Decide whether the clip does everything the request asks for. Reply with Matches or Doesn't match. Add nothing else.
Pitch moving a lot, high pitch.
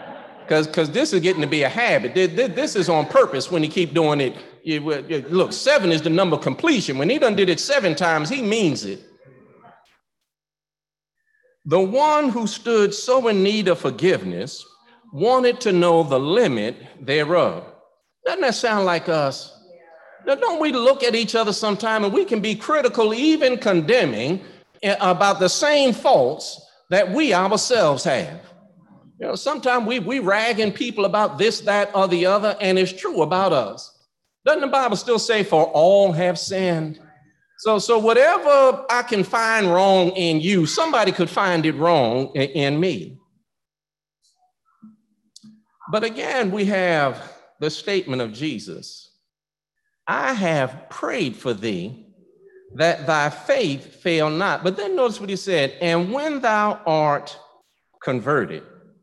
Matches